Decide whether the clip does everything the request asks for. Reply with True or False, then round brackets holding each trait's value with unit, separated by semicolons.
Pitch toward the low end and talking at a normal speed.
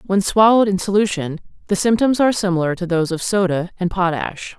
False (190 Hz; 185 wpm)